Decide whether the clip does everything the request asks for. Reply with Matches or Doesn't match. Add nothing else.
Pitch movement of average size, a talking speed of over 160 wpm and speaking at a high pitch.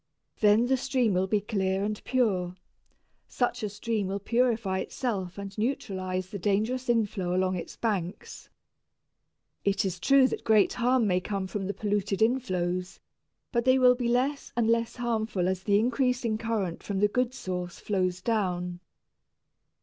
Doesn't match